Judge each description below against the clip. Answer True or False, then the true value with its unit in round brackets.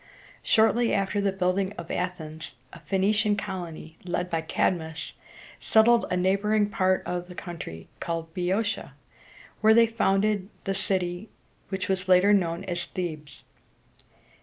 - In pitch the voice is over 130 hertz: True (185 Hz)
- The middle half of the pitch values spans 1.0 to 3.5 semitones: True (2.7 semitones)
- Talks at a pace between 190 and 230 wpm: False (135 wpm)